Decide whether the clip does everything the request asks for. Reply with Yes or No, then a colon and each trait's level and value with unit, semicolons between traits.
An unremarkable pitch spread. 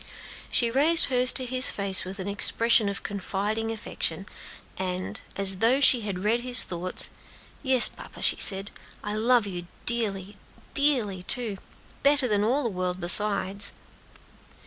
Yes: average, 4.1 semitones